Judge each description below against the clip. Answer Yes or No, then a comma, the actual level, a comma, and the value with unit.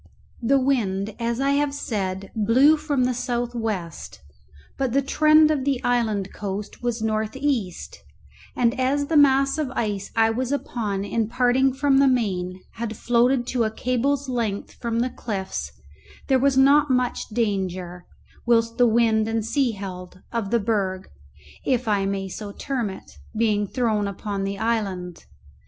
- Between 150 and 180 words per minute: Yes, average, 160 wpm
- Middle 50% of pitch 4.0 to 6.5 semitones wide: Yes, average, 4.4 semitones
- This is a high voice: Yes, high, 230 Hz